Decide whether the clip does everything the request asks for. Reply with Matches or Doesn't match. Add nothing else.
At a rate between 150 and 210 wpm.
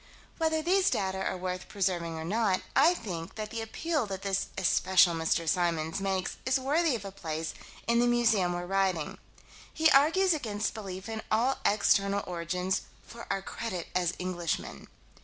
Matches